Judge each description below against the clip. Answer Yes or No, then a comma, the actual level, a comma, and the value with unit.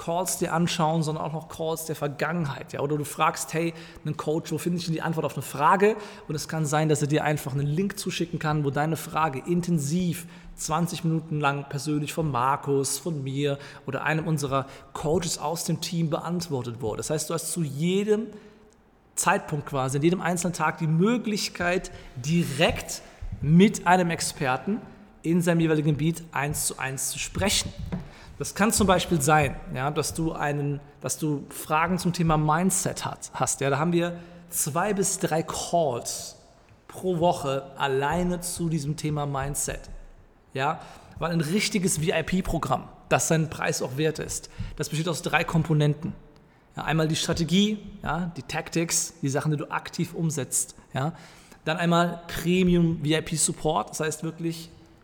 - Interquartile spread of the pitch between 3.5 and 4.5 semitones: No, average, 2.8 semitones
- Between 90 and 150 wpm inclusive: No, average, 170 wpm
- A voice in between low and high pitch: Yes, medium, 160 Hz